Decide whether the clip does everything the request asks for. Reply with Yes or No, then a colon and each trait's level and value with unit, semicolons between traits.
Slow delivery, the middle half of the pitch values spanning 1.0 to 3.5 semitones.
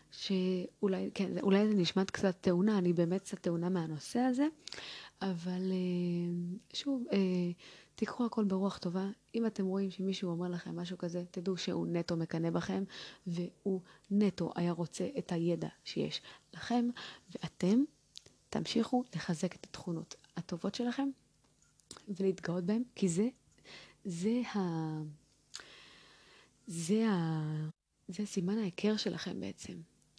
No: average, 120 wpm; average, 2.8 semitones